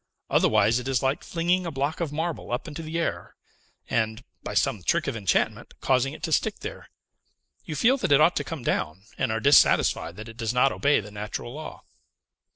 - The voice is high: No, low, 135 Hz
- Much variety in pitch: Yes, wide, 5.8 semitones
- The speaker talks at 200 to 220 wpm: Yes, fast, 205 wpm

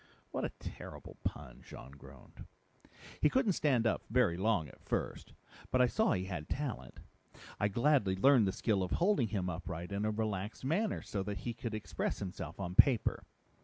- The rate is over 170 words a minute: Yes, average, 180 wpm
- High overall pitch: No, low, 105 Hz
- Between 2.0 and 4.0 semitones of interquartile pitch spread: No, wide, 5.6 semitones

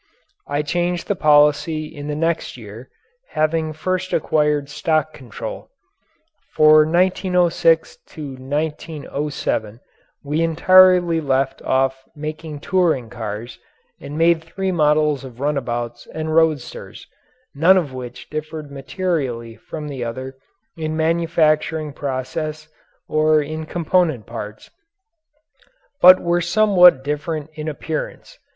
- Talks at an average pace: No, slow, 110 wpm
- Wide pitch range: No, average, 3.0 semitones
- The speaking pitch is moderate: Yes, medium, 155 Hz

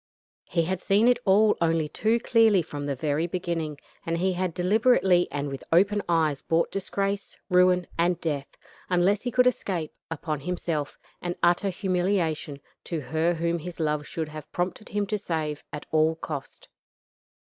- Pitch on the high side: No, medium, 175 Hz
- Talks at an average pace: Yes, average, 165 wpm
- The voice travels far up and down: No, average, 3.6 semitones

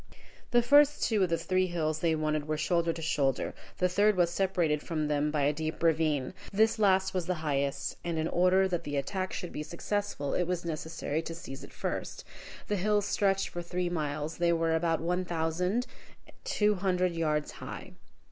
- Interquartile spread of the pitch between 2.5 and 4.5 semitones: Yes, average, 3.2 semitones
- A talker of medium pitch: Yes, medium, 170 Hz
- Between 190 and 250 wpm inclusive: Yes, average, 195 wpm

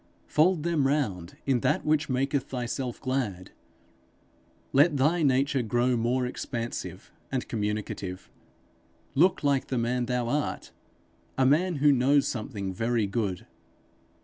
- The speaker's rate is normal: No, slow, 125 wpm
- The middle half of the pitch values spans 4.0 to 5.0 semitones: No, average, 3.5 semitones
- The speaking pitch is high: No, low, 130 Hz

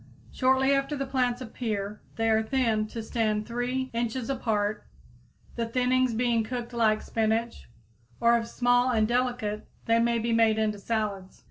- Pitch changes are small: Yes, narrow, 2.3 semitones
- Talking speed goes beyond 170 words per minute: No, average, 155 wpm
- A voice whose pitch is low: No, high, 230 Hz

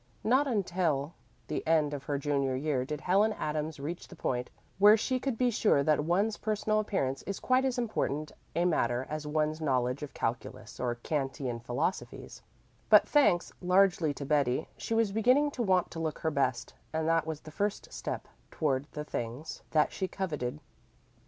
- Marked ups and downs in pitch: Yes, wide, 6.1 semitones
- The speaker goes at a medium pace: Yes, average, 180 wpm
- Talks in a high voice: No, medium, 155 Hz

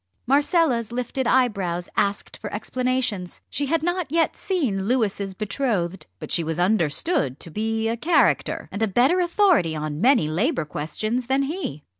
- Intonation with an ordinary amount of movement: No, wide, 7.4 semitones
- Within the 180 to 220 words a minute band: No, average, 155 wpm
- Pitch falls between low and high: No, high, 230 Hz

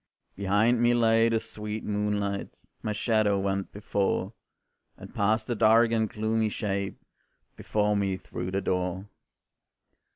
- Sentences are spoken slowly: Yes, slow, 130 wpm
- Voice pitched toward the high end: No, low, 105 Hz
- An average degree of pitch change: No, narrow, 2.0 semitones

